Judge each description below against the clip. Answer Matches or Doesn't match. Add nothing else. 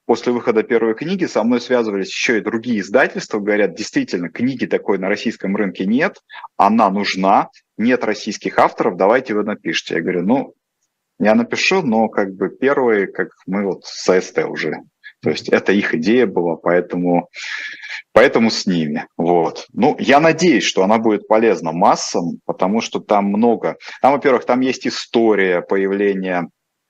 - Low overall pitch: Matches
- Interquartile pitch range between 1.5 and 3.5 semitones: Doesn't match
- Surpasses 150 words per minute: Matches